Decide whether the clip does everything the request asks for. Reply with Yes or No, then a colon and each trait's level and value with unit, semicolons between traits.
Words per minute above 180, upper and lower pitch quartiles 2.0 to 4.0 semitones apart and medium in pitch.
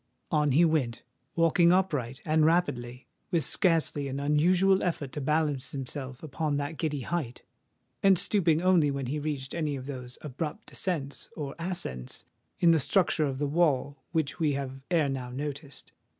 No: average, 150 wpm; average, 3.6 semitones; medium, 150 Hz